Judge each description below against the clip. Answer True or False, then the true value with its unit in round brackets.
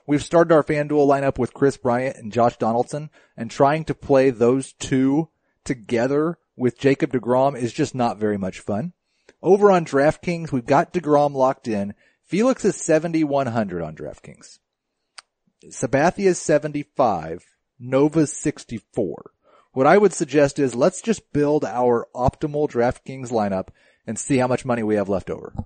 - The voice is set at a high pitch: False (140 Hz)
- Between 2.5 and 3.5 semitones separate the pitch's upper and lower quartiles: False (4.3 semitones)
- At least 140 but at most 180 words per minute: True (165 wpm)